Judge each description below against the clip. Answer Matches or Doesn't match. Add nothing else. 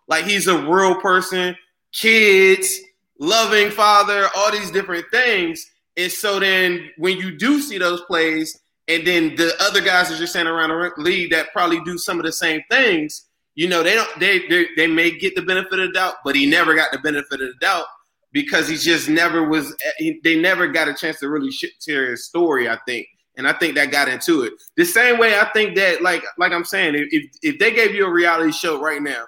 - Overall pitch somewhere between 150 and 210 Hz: Matches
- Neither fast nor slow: Doesn't match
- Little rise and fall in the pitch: Doesn't match